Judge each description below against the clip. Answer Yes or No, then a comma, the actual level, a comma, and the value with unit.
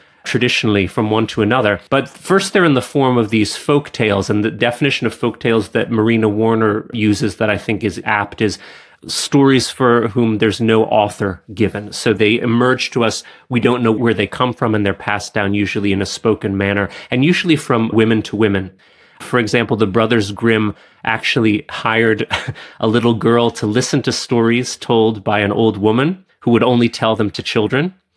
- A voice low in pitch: Yes, low, 115 Hz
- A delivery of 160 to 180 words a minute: No, average, 195 wpm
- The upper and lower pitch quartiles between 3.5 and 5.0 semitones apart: No, narrow, 2.4 semitones